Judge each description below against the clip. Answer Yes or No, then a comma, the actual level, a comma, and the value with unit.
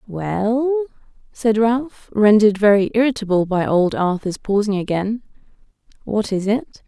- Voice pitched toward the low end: No, high, 215 Hz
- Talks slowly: Yes, slow, 120 wpm